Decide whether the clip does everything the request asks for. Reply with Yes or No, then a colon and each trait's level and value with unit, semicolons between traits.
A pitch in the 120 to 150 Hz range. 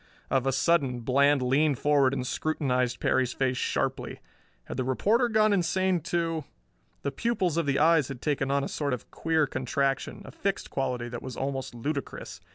Yes: medium, 140 Hz